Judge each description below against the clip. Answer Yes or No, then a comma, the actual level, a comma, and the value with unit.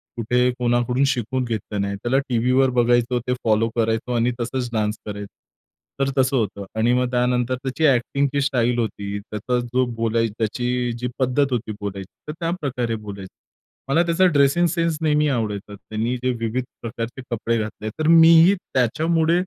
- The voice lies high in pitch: No, low, 125 Hz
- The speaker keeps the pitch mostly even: No, average, 3.3 semitones